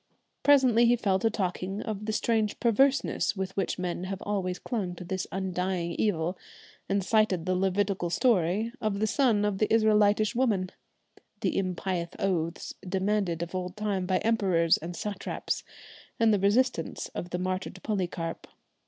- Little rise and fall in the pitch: No, average, 3.0 semitones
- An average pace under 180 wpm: Yes, average, 155 wpm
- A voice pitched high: Yes, high, 195 Hz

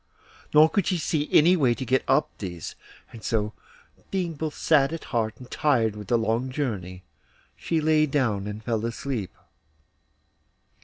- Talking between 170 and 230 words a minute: No, average, 160 wpm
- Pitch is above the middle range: No, low, 130 Hz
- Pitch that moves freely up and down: Yes, wide, 5.8 semitones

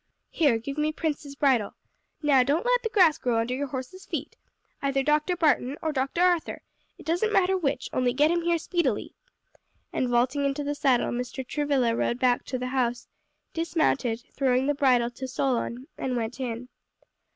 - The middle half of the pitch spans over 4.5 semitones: No, average, 3.8 semitones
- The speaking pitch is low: No, very high, 275 Hz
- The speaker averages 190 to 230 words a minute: No, average, 175 wpm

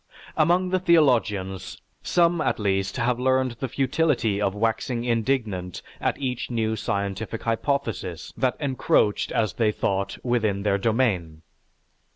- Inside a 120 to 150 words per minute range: Yes, slow, 135 wpm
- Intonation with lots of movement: No, average, 4.7 semitones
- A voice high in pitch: No, low, 115 Hz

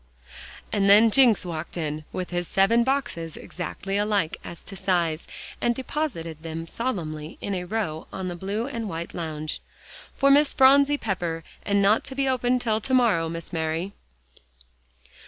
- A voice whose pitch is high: Yes, high, 195 Hz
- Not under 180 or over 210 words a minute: No, average, 160 wpm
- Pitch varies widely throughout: Yes, wide, 6.3 semitones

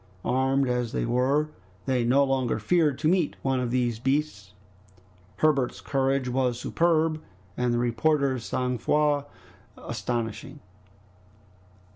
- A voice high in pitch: No, low, 130 Hz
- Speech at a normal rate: No, slow, 120 wpm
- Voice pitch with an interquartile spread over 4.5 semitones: No, average, 3.1 semitones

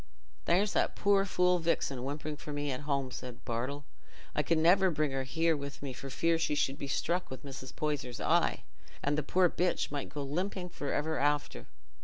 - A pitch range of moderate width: Yes, average, 3.5 semitones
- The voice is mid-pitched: Yes, medium, 145 Hz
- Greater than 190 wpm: Yes, average, 200 wpm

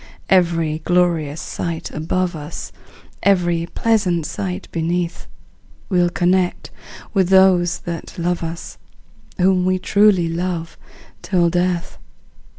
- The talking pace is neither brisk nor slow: No, slow, 105 wpm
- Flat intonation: Yes, narrow, 1.8 semitones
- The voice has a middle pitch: Yes, medium, 175 Hz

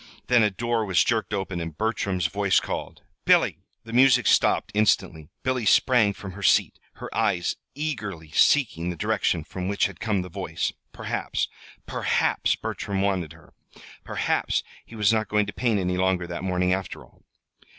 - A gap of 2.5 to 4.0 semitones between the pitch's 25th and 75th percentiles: Yes, average, 3.6 semitones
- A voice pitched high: No, low, 100 Hz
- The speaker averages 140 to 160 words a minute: No, average, 170 wpm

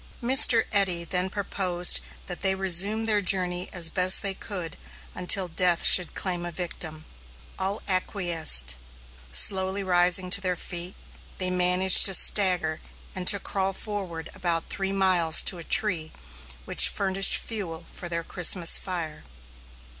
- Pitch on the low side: No, medium, 185 Hz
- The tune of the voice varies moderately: No, narrow, 2.0 semitones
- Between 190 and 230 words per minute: No, average, 140 wpm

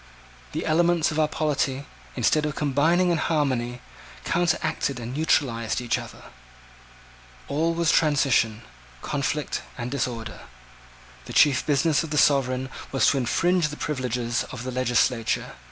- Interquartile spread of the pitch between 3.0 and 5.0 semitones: Yes, average, 3.8 semitones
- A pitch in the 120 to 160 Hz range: Yes, medium, 140 Hz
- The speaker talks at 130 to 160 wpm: Yes, slow, 135 wpm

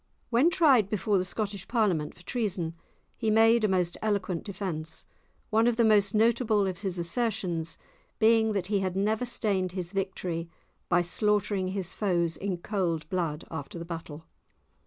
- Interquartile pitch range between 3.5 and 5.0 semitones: Yes, average, 3.8 semitones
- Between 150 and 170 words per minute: Yes, average, 160 wpm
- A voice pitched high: Yes, high, 195 Hz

